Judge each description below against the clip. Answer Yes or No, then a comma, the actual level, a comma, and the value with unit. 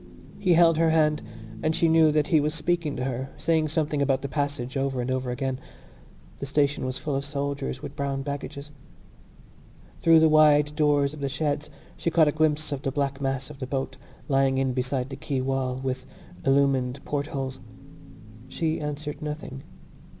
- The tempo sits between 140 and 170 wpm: No, average, 180 wpm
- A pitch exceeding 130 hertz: Yes, medium, 140 Hz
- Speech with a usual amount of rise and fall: No, narrow, 2.2 semitones